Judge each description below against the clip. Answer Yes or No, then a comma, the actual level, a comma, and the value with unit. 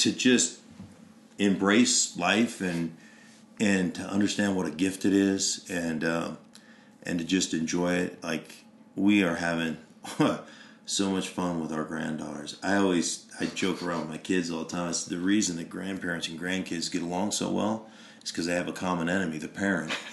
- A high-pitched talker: No, very low, 90 Hz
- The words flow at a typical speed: Yes, average, 180 wpm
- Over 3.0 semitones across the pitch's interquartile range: No, average, 2.7 semitones